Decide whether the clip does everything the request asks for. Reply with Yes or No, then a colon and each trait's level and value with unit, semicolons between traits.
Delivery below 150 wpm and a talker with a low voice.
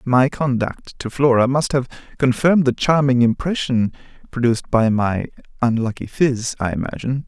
Yes: average, 140 wpm; low, 125 Hz